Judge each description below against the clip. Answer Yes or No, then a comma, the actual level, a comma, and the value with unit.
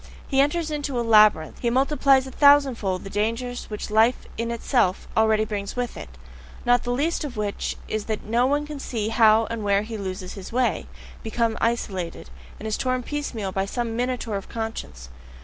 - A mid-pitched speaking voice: No, high, 230 Hz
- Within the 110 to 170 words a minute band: No, average, 185 wpm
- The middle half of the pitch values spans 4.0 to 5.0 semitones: No, average, 3.3 semitones